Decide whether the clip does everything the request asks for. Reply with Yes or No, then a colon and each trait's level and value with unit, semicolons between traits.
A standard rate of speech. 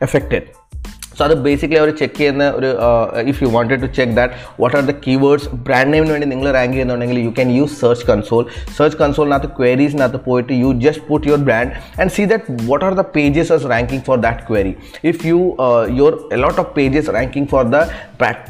No: fast, 195 wpm